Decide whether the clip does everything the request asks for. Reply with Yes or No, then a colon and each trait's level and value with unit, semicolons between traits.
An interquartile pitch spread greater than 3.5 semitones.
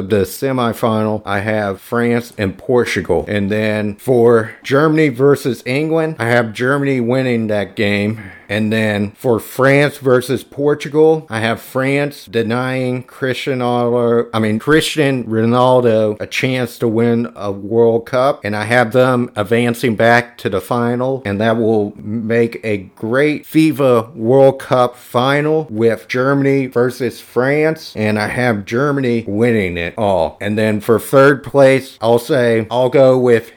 No: average, 3.2 semitones